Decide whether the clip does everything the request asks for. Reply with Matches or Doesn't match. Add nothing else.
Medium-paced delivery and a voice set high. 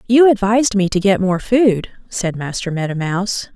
Matches